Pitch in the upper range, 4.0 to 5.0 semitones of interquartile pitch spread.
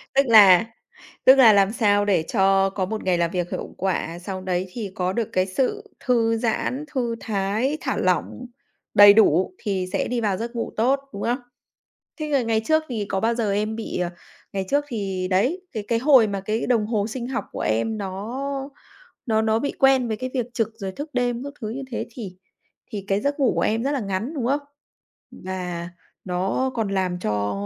Yes: high, 220 Hz; average, 4.3 semitones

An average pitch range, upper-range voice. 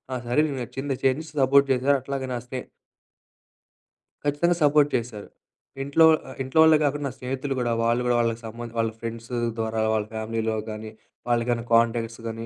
No: average, 3.3 semitones; low, 125 Hz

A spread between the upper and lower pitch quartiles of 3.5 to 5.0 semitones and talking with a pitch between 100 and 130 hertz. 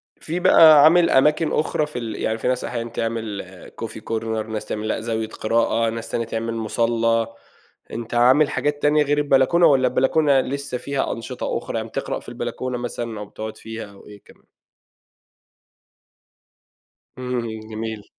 Yes: average, 3.9 semitones; low, 115 Hz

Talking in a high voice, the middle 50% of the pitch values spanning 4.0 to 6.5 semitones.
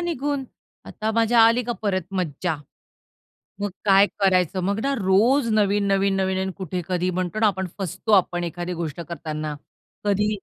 No: high, 195 Hz; average, 3.1 semitones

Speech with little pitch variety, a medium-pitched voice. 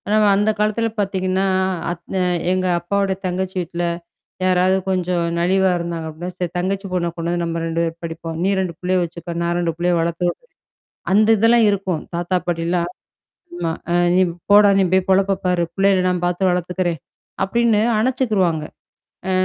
Yes: narrow, 2.1 semitones; medium, 180 Hz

